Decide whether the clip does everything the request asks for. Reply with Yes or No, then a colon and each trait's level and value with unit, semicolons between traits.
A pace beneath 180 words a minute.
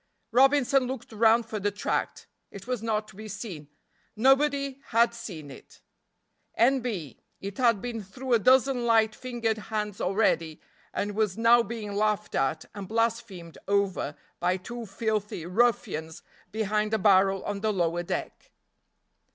Yes: average, 150 wpm